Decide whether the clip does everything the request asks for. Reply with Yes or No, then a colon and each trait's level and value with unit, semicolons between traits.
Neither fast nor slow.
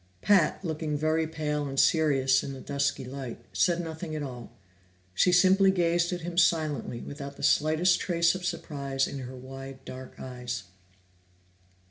Yes: average, 155 wpm